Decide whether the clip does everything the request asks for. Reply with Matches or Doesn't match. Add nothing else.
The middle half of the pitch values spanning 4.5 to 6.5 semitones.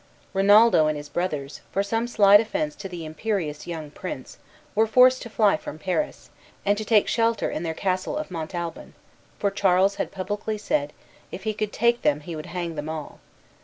Matches